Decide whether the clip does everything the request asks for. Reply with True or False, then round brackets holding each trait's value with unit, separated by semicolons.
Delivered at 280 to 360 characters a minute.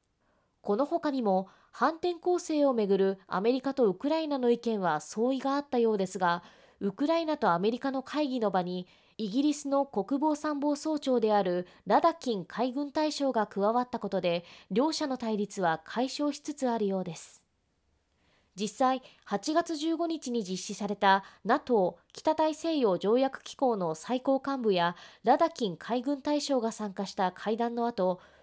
True (310 characters per minute)